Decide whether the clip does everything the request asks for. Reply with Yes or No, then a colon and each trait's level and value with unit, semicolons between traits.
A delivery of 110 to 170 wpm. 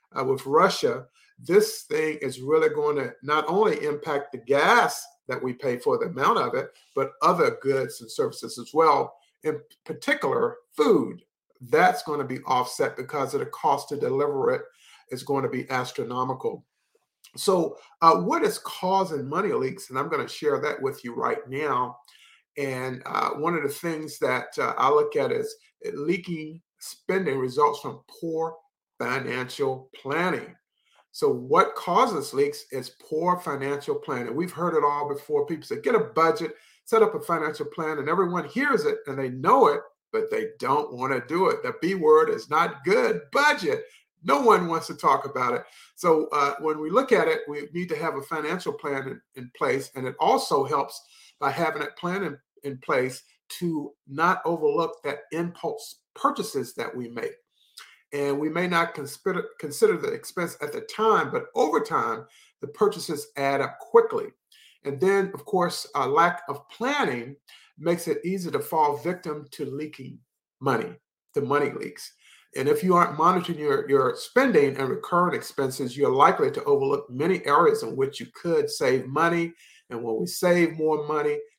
No: average, 180 wpm